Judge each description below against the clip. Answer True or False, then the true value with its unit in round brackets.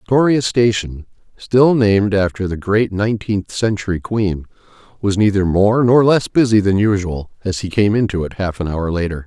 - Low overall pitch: True (100 Hz)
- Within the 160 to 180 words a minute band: True (175 wpm)